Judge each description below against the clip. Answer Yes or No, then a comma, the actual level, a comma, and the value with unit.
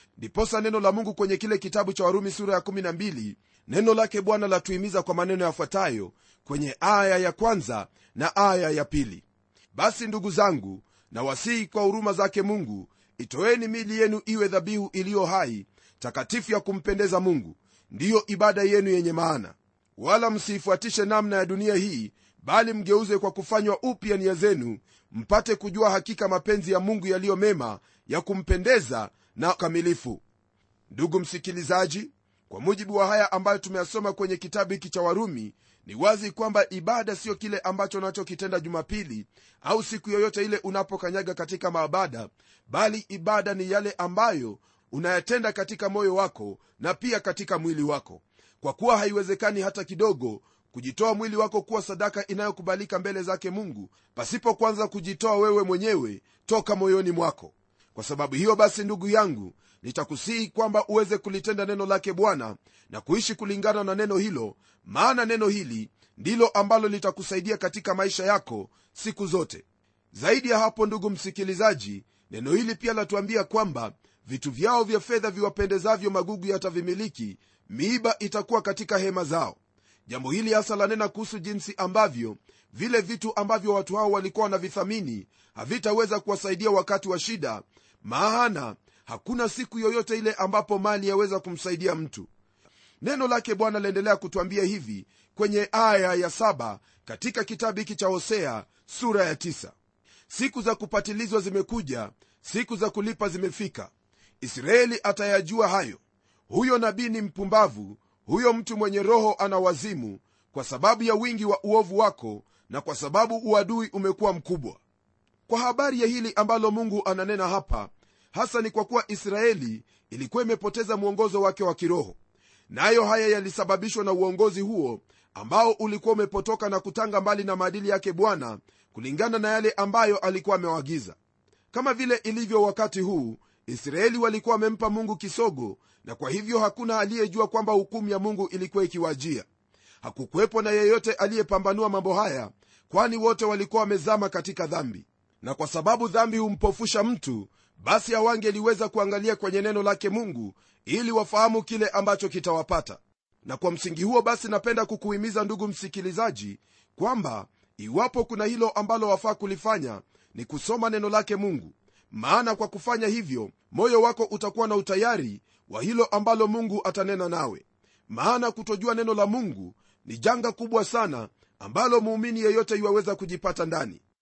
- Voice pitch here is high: Yes, high, 200 Hz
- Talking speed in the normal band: No, fast, 145 wpm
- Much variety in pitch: No, average, 3.2 semitones